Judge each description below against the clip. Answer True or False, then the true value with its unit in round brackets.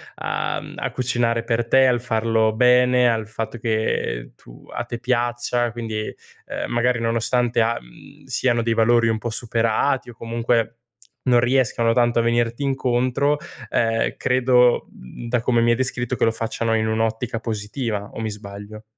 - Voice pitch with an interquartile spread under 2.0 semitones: True (1.4 semitones)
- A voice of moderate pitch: False (115 Hz)